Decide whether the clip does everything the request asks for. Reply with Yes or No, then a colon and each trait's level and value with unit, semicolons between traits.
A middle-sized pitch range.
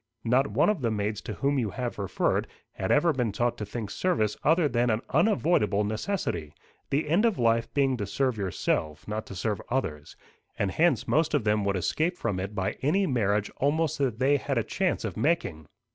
No: wide, 6.1 semitones